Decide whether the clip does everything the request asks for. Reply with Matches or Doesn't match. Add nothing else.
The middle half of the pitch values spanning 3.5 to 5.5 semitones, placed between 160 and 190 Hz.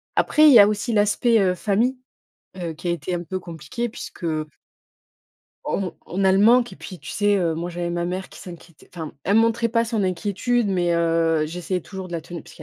Matches